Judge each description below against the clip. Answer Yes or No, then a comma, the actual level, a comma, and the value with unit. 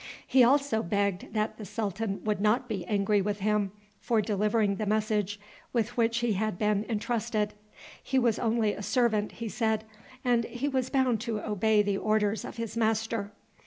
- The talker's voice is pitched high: Yes, high, 215 Hz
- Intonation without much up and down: Yes, narrow, 2.0 semitones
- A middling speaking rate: Yes, average, 175 wpm